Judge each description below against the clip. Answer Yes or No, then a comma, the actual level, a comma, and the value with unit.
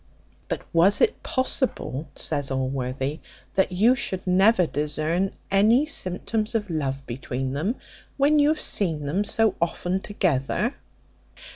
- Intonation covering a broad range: Yes, wide, 7.3 semitones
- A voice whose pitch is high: No, medium, 180 Hz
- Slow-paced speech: Yes, slow, 130 wpm